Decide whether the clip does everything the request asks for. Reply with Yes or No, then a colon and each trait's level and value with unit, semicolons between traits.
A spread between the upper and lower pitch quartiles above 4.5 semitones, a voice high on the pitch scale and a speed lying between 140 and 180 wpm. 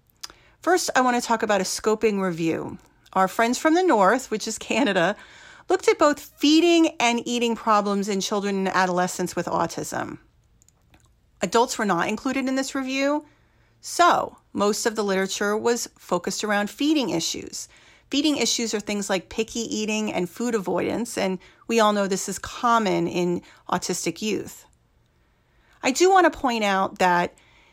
Yes: wide, 5.4 semitones; high, 215 Hz; average, 160 wpm